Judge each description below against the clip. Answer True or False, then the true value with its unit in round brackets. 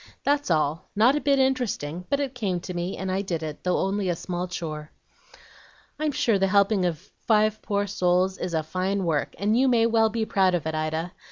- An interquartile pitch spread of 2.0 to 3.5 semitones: False (4.1 semitones)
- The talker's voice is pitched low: False (190 Hz)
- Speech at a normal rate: False (215 wpm)